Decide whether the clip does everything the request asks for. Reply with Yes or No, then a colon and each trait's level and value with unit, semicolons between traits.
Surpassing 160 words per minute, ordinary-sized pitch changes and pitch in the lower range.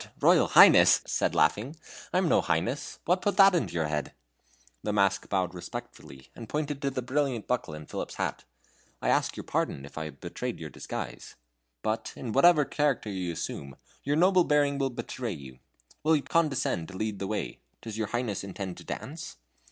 No: average, 190 wpm; wide, 8.2 semitones; low, 115 Hz